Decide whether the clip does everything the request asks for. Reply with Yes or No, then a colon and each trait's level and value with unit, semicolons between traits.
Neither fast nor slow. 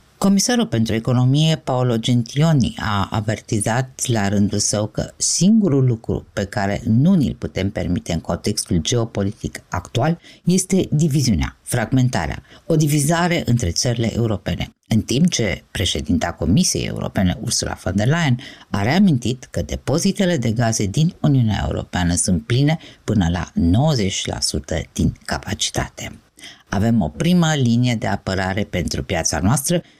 Yes: average, 130 wpm